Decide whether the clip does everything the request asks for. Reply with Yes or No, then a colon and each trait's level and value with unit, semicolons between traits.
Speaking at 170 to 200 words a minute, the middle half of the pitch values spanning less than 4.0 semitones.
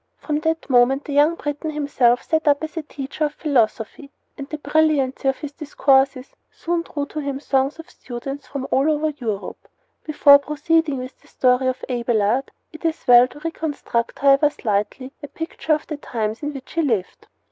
Yes: average, 185 wpm; average, 3.1 semitones